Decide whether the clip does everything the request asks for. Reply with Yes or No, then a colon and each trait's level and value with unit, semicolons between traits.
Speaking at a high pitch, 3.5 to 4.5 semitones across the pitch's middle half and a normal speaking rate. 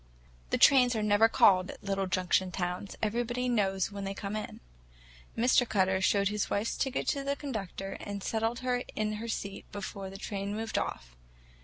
No: high, 205 Hz; average, 3.0 semitones; average, 180 wpm